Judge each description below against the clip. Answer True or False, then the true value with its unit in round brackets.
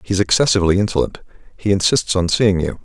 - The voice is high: False (95 Hz)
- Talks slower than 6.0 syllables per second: False (6.3 syllables/s)